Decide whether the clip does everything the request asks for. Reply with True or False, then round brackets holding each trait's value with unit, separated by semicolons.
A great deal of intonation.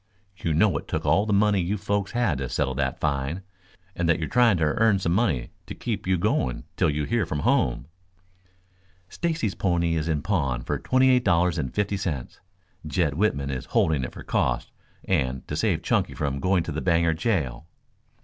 True (6.0 semitones)